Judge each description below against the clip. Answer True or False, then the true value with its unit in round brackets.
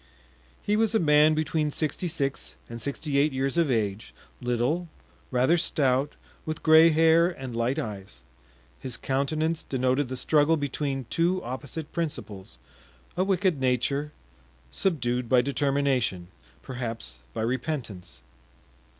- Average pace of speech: False (125 wpm)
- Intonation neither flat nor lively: True (4.4 semitones)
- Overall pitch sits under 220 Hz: True (140 Hz)